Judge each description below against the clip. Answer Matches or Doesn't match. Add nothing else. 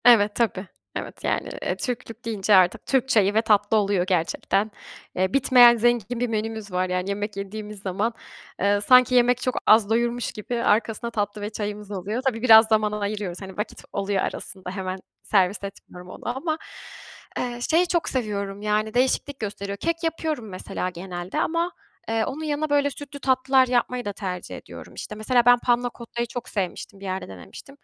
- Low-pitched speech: Doesn't match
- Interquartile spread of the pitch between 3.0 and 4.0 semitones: Matches